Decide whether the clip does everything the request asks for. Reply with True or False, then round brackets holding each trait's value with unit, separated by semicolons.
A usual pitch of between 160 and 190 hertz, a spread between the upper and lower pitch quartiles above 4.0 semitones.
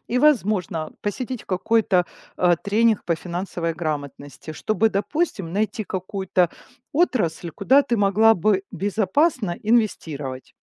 False (200 Hz; 4.4 semitones)